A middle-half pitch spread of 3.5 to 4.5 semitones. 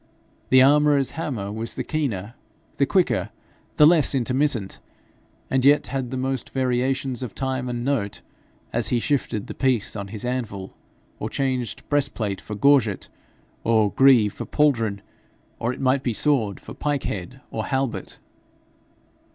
Yes: average, 3.8 semitones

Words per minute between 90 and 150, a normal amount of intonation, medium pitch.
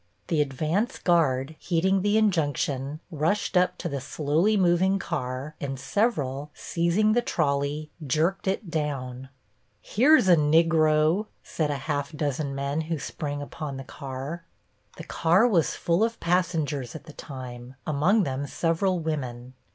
Yes: average, 145 wpm; average, 4.1 semitones; medium, 155 Hz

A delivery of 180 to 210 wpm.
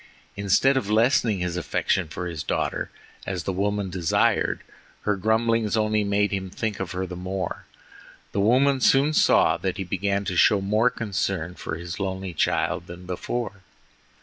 No: average, 165 wpm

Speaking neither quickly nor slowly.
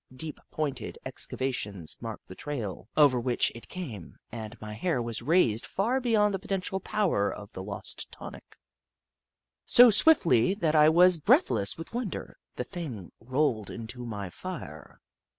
Yes: average, 150 wpm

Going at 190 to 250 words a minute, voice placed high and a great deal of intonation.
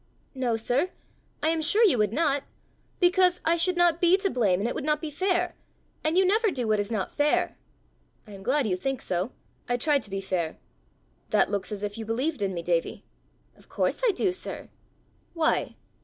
Yes: fast, 205 wpm; very high, 275 Hz; wide, 8.9 semitones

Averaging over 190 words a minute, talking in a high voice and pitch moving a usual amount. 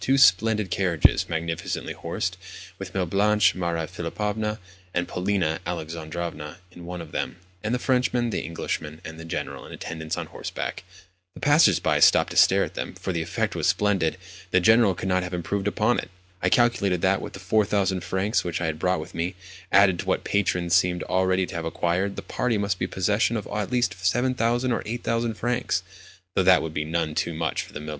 No: average, 200 wpm; very low, 95 Hz; average, 3.6 semitones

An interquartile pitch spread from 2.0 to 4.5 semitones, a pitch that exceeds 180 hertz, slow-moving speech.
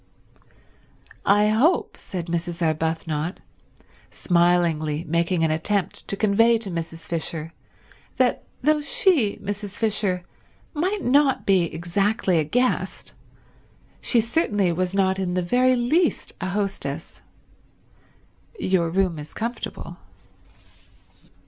No: average, 5.2 semitones; high, 190 Hz; slow, 110 wpm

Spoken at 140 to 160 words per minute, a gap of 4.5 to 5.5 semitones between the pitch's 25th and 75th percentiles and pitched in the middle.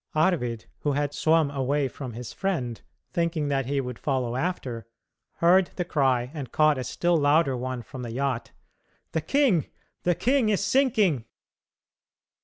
Yes: average, 155 wpm; average, 5.2 semitones; medium, 145 Hz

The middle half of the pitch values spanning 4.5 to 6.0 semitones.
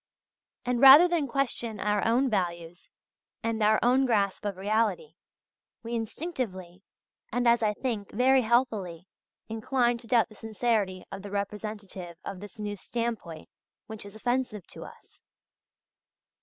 No: average, 3.3 semitones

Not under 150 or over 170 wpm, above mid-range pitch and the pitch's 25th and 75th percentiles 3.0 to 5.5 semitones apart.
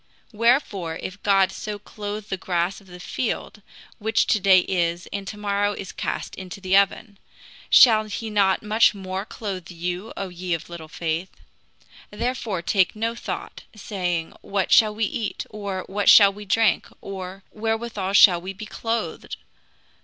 No: average, 160 wpm; high, 200 Hz; narrow, 2.5 semitones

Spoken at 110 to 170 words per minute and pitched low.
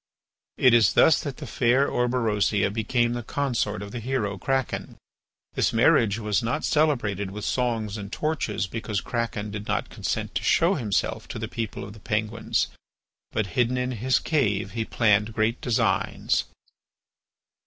Yes: average, 155 wpm; low, 115 Hz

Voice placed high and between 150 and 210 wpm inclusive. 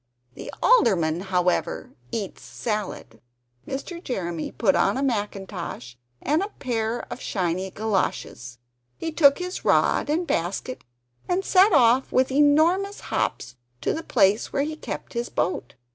No: high, 235 Hz; average, 140 wpm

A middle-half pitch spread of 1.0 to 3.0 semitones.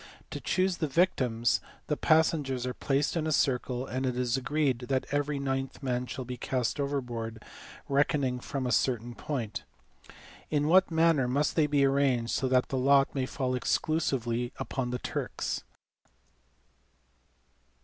Yes: average, 2.7 semitones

